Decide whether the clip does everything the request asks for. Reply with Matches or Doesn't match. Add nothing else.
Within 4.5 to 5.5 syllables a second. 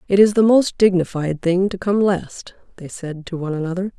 Matches